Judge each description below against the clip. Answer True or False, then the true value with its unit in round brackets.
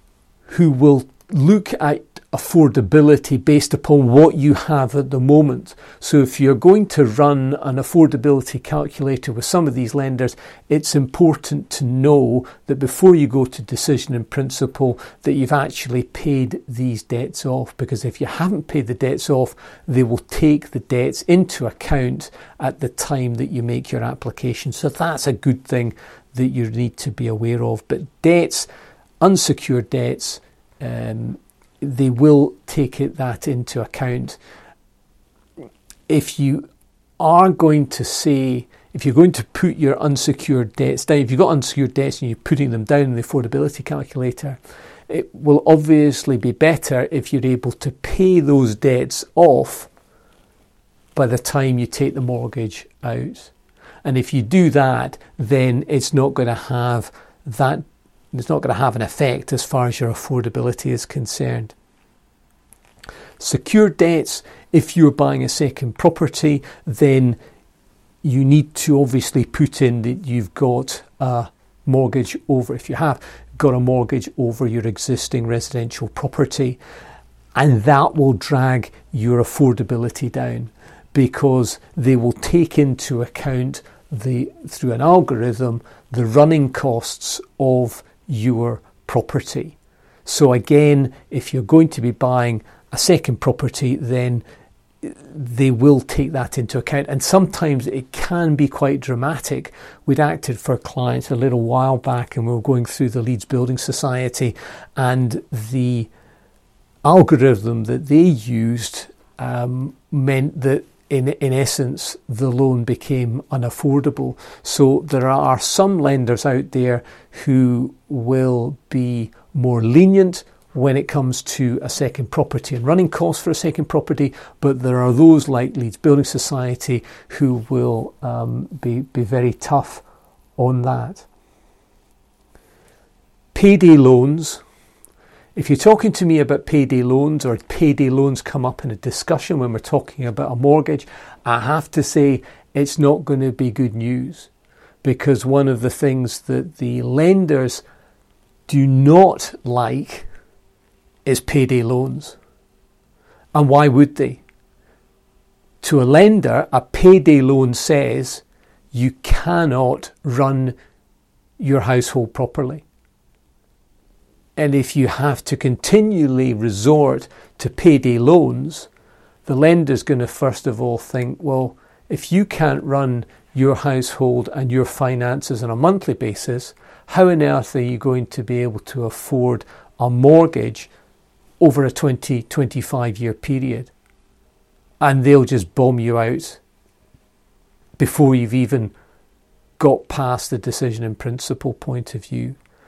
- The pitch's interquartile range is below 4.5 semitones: True (2.8 semitones)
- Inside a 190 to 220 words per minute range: False (145 wpm)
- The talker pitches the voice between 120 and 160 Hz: True (135 Hz)